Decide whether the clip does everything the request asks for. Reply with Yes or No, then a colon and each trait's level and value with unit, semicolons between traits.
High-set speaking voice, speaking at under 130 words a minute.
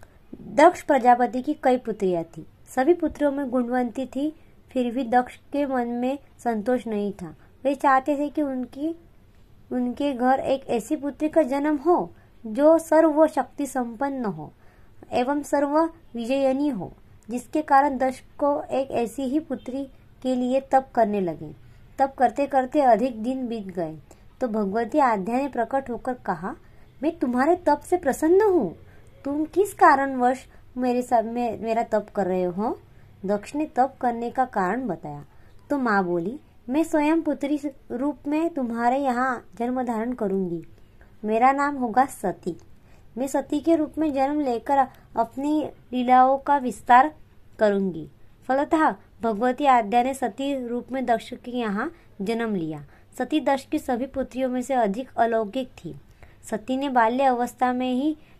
No: very high, 255 Hz; average, 155 wpm